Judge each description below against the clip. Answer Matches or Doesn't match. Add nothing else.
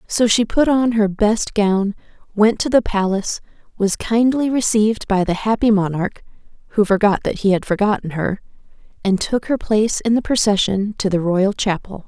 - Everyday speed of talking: Matches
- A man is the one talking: Doesn't match